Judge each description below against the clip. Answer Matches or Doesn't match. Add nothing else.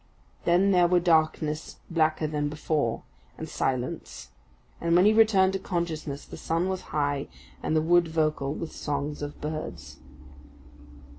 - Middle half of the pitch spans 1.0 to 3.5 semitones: Matches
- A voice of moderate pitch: Matches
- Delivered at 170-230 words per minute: Doesn't match